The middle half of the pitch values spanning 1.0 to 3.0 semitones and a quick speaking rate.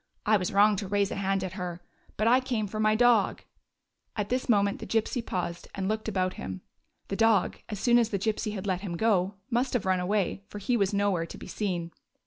Yes: average, 2.7 semitones; fast, 235 wpm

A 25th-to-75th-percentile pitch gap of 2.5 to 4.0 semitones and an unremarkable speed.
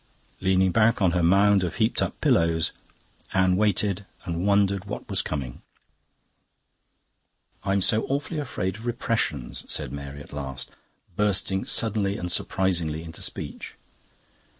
No: average, 3.7 semitones; slow, 130 wpm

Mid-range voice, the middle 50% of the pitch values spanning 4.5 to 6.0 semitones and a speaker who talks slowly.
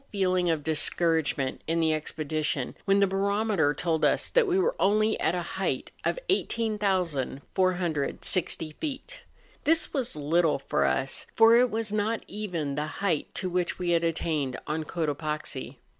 No: medium, 175 Hz; average, 5.3 semitones; average, 150 wpm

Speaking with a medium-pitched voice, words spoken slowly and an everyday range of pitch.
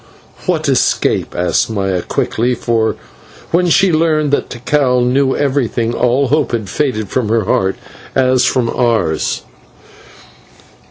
No: low, 125 Hz; slow, 125 wpm; average, 4.0 semitones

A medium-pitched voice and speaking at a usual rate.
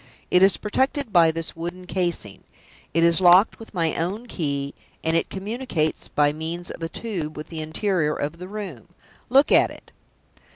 Yes: medium, 170 Hz; average, 175 wpm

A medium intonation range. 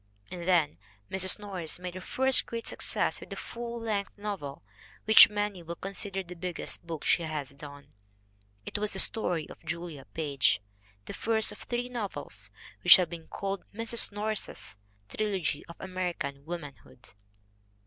Yes: average, 4.4 semitones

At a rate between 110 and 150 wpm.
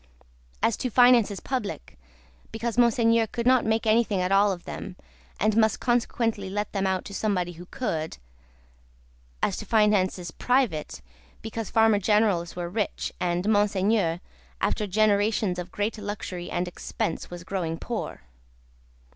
Yes: average, 140 wpm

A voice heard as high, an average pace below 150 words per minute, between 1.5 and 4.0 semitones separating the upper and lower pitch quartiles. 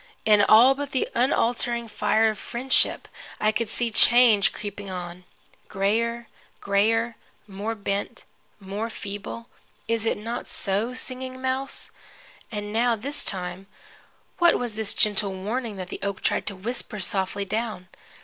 Yes: high, 220 Hz; average, 140 wpm; average, 3.0 semitones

